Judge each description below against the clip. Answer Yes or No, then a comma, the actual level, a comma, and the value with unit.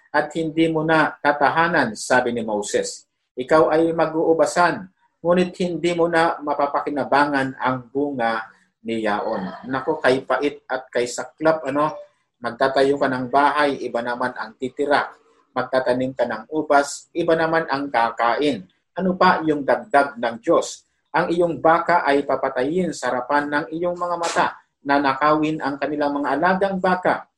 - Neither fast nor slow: Yes, average, 145 wpm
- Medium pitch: Yes, medium, 145 Hz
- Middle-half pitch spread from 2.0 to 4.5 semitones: Yes, average, 4.0 semitones